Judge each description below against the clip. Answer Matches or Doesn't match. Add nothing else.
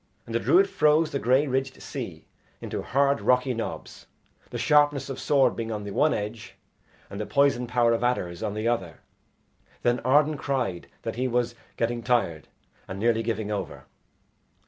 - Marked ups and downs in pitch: Doesn't match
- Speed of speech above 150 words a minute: Matches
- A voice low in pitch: Matches